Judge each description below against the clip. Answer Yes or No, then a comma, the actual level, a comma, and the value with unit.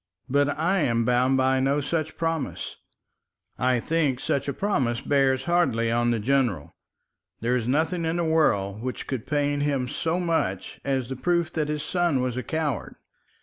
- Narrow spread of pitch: No, average, 4.3 semitones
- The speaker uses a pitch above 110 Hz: Yes, low, 135 Hz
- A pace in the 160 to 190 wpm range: Yes, average, 170 wpm